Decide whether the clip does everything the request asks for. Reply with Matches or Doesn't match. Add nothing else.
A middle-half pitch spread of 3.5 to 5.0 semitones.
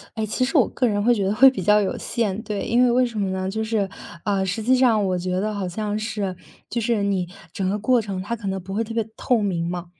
Doesn't match